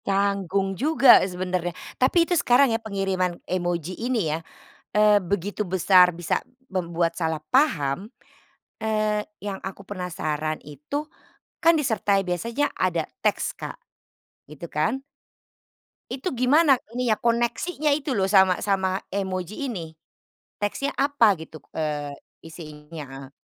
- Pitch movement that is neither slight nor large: No, wide, 5.7 semitones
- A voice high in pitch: Yes, high, 195 Hz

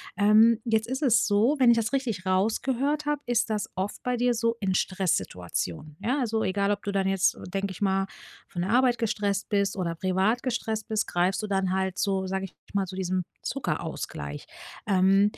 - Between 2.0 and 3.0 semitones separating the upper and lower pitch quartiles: No, average, 3.4 semitones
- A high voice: Yes, high, 200 Hz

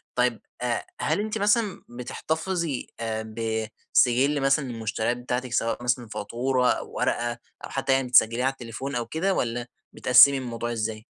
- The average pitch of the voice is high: No, low, 125 Hz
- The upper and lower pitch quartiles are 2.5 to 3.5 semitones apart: Yes, average, 2.9 semitones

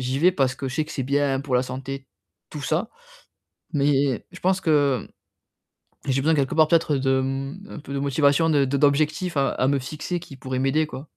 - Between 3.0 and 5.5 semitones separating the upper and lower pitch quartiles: No, narrow, 2.6 semitones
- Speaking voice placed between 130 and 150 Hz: Yes, medium, 140 Hz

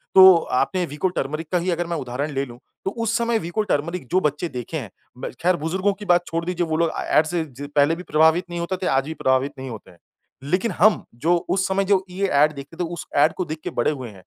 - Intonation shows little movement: No, average, 4.3 semitones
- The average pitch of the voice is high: No, medium, 165 Hz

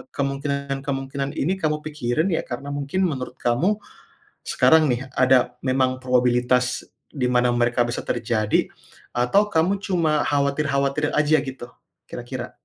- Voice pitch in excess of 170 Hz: No, low, 135 Hz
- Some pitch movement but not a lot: Yes, average, 3.1 semitones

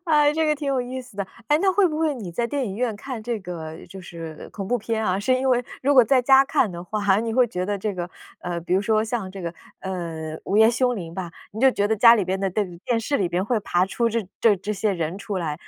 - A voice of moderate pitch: No, high, 215 Hz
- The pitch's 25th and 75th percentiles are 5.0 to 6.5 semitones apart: Yes, average, 5.3 semitones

